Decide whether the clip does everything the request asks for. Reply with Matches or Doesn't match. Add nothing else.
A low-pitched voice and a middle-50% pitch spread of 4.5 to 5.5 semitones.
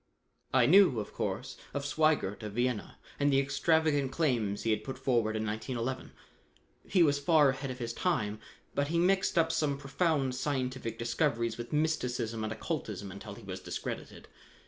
Matches